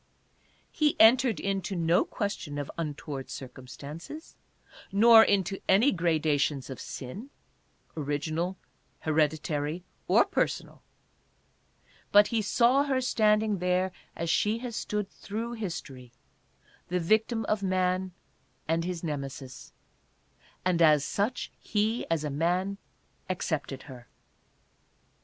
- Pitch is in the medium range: Yes, medium, 180 Hz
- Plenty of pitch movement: Yes, wide, 5.7 semitones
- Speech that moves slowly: Yes, slow, 115 wpm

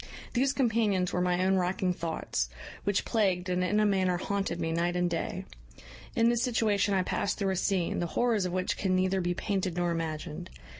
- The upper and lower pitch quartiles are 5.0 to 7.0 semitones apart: No, narrow, 2.4 semitones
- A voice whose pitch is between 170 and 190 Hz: Yes, medium, 185 Hz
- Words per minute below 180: No, average, 200 wpm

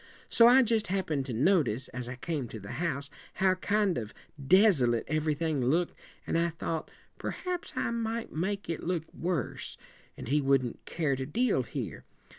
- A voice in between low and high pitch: Yes, medium, 165 Hz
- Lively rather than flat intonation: Yes, wide, 6.4 semitones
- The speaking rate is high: No, average, 170 wpm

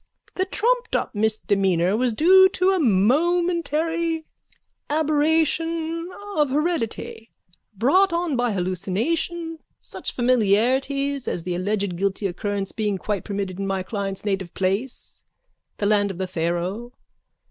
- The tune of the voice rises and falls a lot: Yes, wide, 8.7 semitones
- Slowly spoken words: Yes, slow, 125 wpm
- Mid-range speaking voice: No, high, 235 Hz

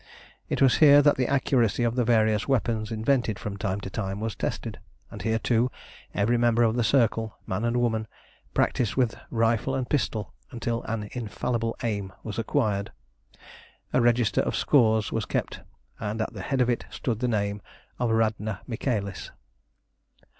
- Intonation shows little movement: Yes, narrow, 2.3 semitones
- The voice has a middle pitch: No, low, 115 Hz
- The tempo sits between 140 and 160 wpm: No, average, 170 wpm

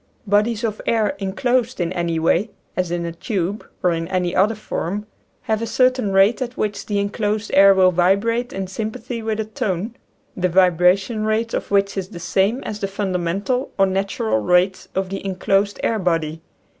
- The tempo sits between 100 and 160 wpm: No, average, 185 wpm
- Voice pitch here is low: No, high, 195 Hz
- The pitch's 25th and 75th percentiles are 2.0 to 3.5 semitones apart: Yes, average, 3.1 semitones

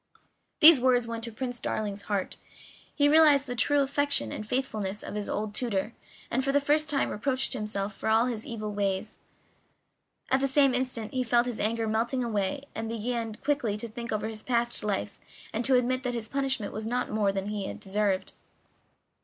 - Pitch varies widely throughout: No, average, 3.6 semitones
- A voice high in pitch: Yes, high, 230 Hz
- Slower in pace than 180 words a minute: No, average, 200 wpm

